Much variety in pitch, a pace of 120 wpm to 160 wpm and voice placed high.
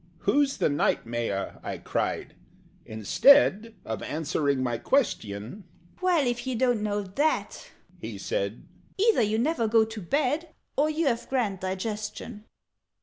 Yes: wide, 8.4 semitones; average, 140 wpm; high, 225 Hz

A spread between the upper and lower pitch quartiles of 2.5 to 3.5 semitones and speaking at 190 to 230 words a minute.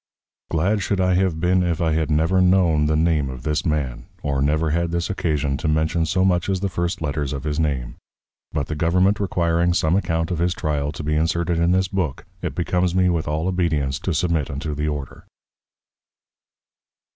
Yes: average, 2.9 semitones; average, 200 wpm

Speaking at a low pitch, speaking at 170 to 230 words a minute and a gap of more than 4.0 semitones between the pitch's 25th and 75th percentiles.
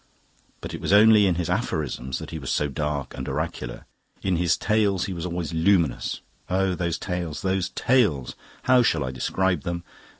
Yes: very low, 85 Hz; average, 180 wpm; average, 4.5 semitones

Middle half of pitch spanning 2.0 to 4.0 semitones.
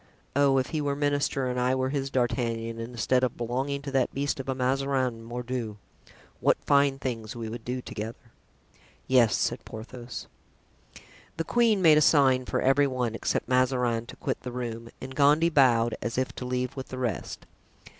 Yes: narrow, 2.5 semitones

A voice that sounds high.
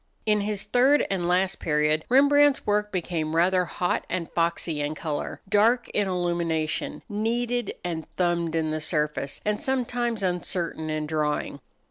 No: medium, 180 Hz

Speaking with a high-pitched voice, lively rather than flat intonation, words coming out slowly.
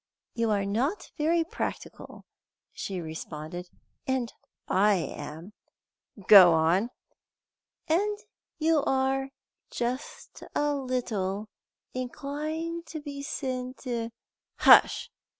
Yes: very high, 255 Hz; wide, 6.8 semitones; slow, 95 wpm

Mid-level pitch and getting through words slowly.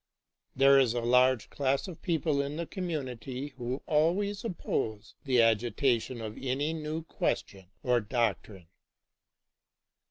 No: low, 130 Hz; slow, 130 wpm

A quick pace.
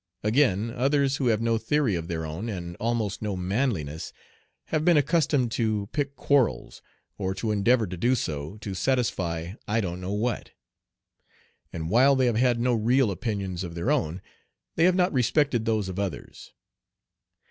No: average, 170 wpm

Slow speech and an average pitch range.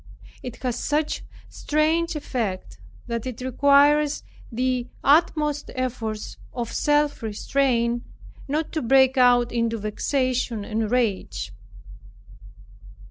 Yes: slow, 100 wpm; average, 3.9 semitones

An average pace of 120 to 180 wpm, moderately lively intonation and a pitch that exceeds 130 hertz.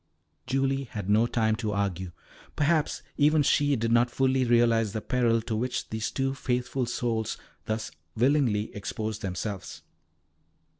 No: average, 140 wpm; average, 3.4 semitones; low, 115 Hz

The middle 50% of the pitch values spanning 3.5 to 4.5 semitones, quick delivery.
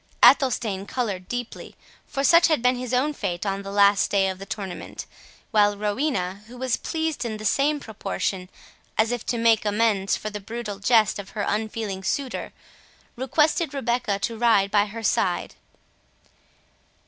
No: average, 3.8 semitones; average, 160 wpm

